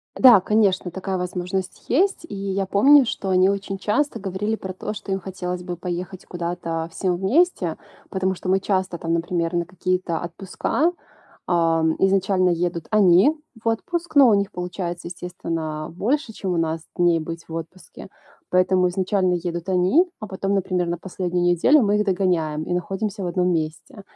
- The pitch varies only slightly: Yes, narrow, 2.2 semitones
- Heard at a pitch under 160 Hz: No, medium, 185 Hz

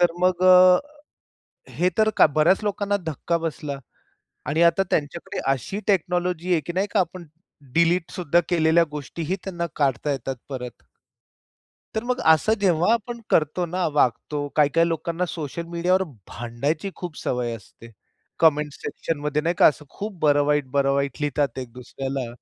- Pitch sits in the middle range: Yes, medium, 165 Hz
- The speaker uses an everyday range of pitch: Yes, average, 4.0 semitones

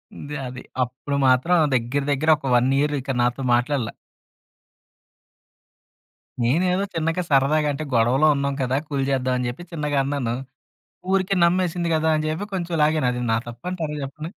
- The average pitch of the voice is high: No, medium, 145 Hz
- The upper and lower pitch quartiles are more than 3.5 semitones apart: Yes, average, 4.2 semitones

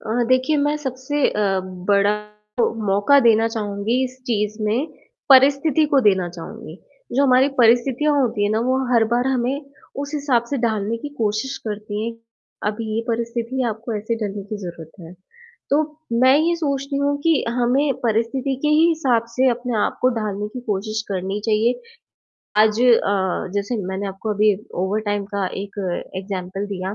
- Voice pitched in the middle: No, high, 230 Hz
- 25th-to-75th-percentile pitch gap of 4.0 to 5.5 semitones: Yes, average, 4.3 semitones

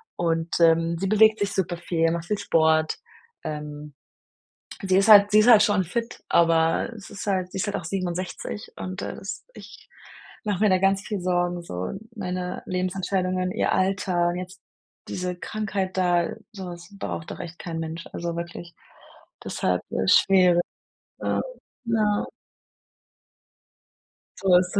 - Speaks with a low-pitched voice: No, medium, 180 Hz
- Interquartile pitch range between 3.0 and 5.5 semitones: No, narrow, 2.5 semitones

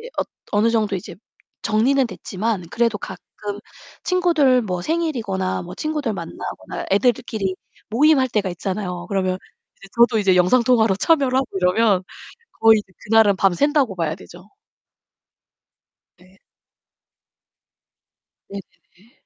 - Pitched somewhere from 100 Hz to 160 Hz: No, high, 215 Hz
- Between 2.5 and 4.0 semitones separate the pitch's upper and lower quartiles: No, average, 5.2 semitones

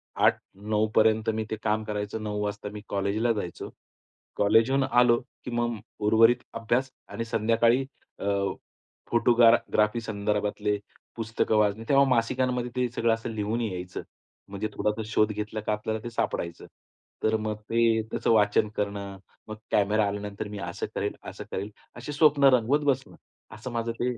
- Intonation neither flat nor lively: No, narrow, 2.1 semitones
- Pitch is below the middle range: Yes, low, 110 Hz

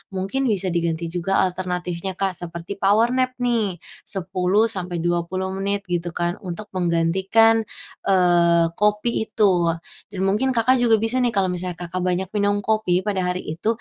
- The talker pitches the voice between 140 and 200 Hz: Yes, high, 190 Hz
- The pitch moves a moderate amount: Yes, average, 3.3 semitones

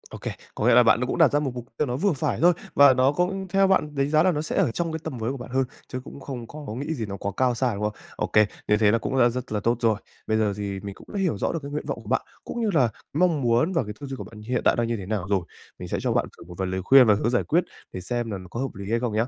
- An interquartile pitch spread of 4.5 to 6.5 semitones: Yes, average, 5.3 semitones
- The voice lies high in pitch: No, low, 125 Hz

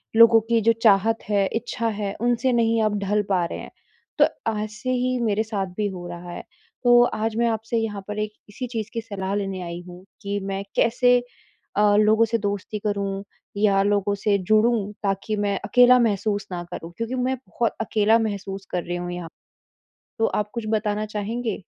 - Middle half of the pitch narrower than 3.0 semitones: Yes, narrow, 2.4 semitones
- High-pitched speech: Yes, high, 210 Hz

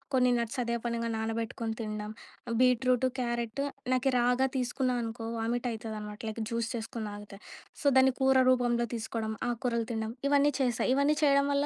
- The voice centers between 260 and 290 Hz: No, high, 235 Hz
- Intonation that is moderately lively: No, narrow, 2.2 semitones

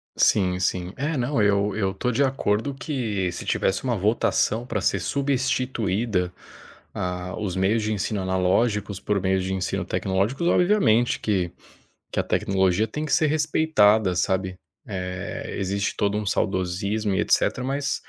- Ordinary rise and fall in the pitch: Yes, average, 4.4 semitones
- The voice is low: Yes, low, 105 Hz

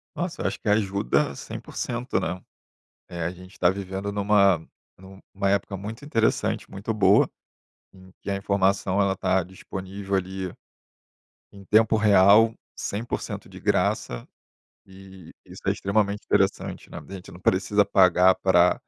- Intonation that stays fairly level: Yes, narrow, 1.5 semitones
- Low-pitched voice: Yes, very low, 95 Hz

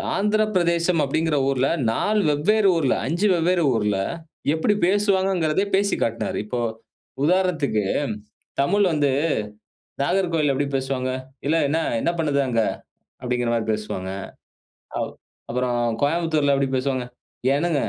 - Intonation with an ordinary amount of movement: No, wide, 6.0 semitones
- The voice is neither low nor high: Yes, medium, 155 Hz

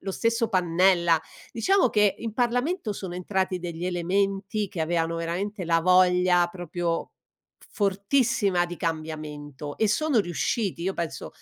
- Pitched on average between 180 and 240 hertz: Yes, medium, 185 Hz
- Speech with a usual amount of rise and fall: Yes, average, 3.4 semitones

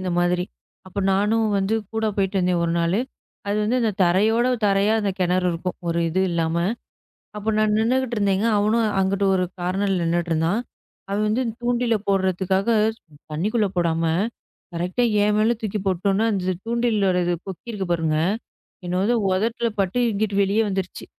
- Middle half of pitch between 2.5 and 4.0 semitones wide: Yes, average, 3.3 semitones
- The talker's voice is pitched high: Yes, high, 195 Hz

